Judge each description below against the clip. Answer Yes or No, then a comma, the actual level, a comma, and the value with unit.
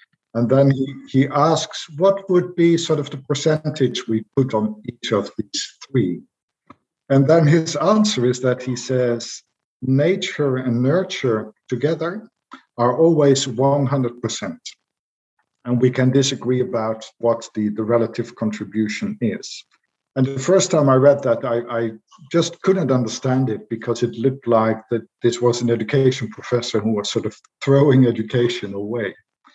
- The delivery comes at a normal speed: Yes, average, 150 wpm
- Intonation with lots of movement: No, average, 3.9 semitones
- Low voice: Yes, low, 130 Hz